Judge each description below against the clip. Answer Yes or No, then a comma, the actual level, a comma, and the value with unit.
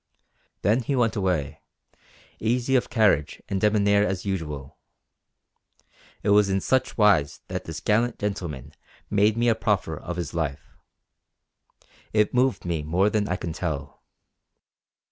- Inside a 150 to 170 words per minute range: No, average, 140 wpm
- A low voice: Yes, low, 100 Hz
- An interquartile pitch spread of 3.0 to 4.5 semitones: No, average, 5.0 semitones